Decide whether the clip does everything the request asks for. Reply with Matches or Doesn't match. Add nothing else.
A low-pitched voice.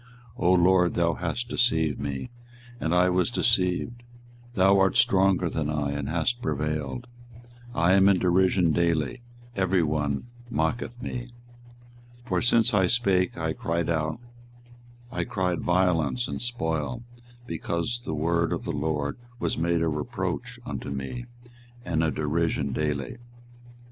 Matches